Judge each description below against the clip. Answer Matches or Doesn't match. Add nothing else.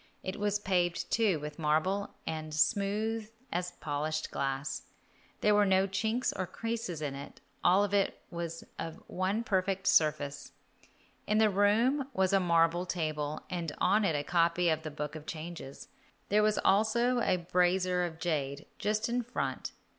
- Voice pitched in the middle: Matches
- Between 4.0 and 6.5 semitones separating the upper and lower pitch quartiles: Matches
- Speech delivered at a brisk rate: Doesn't match